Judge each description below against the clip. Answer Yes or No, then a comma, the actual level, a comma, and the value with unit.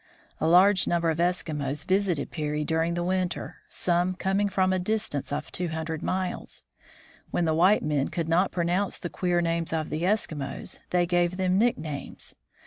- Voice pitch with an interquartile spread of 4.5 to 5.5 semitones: No, narrow, 2.6 semitones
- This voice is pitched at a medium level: Yes, medium, 175 Hz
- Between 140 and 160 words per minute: No, average, 170 wpm